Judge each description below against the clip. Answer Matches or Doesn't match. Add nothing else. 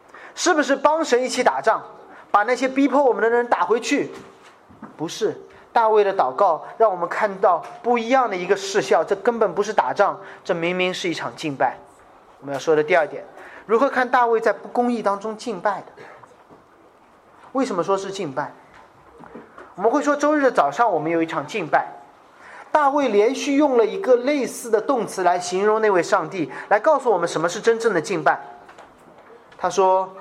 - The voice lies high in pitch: Matches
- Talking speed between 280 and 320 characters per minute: Doesn't match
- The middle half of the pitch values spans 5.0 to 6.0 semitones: Matches